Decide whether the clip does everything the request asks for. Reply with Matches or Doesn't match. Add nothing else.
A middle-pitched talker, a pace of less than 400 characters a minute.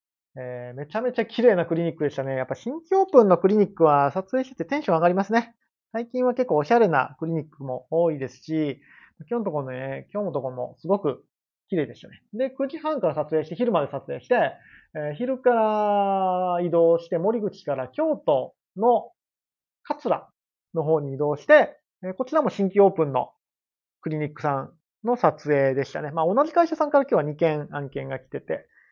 Matches